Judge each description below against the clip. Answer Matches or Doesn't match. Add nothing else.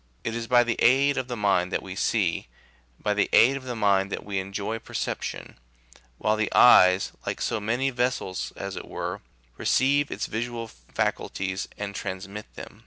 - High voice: Doesn't match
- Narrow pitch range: Doesn't match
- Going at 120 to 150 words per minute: Doesn't match